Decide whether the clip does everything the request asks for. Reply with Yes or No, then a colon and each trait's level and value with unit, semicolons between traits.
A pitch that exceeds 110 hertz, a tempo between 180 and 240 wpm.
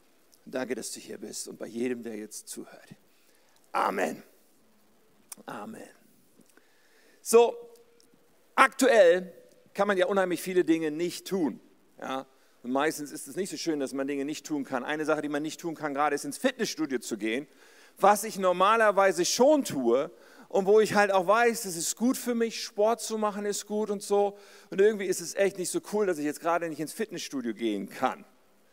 Yes: high, 190 Hz; fast, 190 wpm